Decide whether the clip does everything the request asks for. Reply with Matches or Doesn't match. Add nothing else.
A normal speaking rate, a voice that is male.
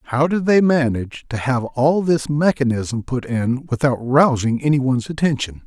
Matches